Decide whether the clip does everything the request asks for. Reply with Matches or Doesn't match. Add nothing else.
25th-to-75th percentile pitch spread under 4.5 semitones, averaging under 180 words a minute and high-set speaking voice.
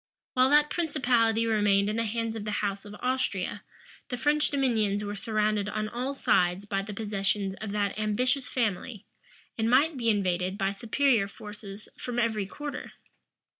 Matches